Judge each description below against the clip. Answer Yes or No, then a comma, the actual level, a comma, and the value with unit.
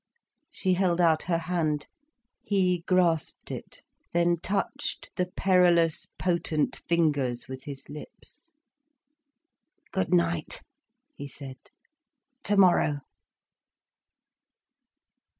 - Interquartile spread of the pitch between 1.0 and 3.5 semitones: Yes, average, 3.2 semitones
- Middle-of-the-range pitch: Yes, medium, 170 Hz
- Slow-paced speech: Yes, slow, 85 wpm